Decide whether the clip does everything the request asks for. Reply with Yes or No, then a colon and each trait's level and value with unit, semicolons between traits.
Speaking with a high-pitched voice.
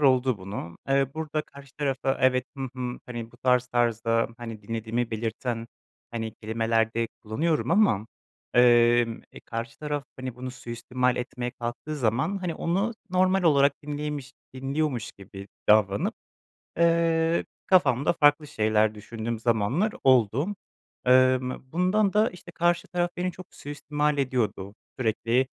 No: low, 130 Hz